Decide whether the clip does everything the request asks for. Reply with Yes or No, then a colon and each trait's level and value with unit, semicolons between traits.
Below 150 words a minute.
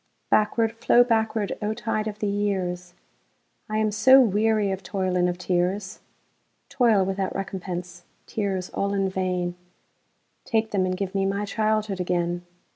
Yes: slow, 135 wpm